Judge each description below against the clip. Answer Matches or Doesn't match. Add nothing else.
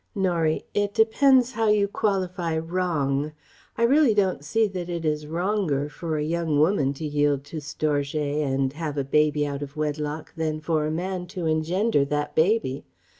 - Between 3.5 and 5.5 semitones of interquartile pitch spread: Matches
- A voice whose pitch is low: Doesn't match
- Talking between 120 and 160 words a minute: Doesn't match